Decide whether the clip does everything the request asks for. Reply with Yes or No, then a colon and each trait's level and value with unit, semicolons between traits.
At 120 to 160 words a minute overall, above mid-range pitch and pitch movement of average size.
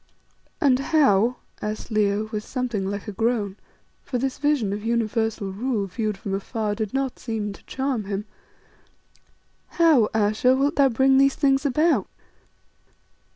Yes: average, 145 wpm; high, 230 Hz; average, 4.4 semitones